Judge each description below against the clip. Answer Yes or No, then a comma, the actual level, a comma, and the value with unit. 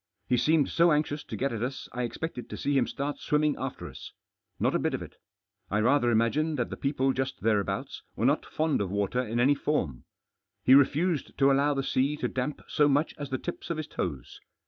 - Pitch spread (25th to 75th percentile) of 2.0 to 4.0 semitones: Yes, average, 3.4 semitones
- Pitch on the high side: No, low, 135 Hz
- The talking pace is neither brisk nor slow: No, fast, 220 wpm